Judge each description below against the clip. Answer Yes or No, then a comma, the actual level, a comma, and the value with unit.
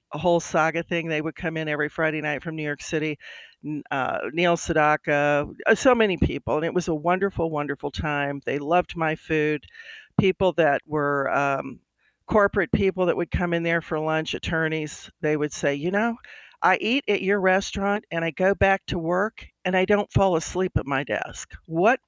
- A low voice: No, medium, 165 Hz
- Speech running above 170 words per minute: Yes, average, 195 wpm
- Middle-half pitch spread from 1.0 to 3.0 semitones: No, average, 3.9 semitones